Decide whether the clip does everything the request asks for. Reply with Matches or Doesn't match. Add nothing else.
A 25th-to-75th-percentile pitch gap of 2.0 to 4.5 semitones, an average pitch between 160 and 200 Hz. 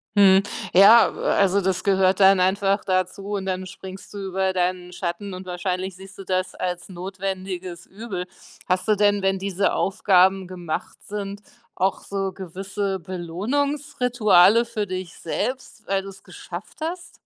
Doesn't match